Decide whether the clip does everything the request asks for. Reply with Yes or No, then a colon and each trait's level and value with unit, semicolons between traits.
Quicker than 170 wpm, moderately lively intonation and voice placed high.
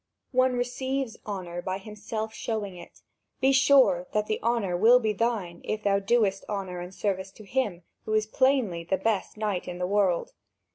Yes: average, 180 wpm; average, 3.8 semitones; high, 210 Hz